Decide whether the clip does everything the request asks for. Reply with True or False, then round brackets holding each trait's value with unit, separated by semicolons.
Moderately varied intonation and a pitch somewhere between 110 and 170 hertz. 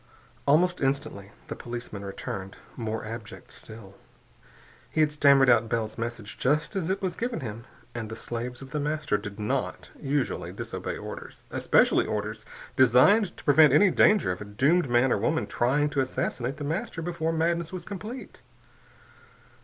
False (6.1 semitones; 135 Hz)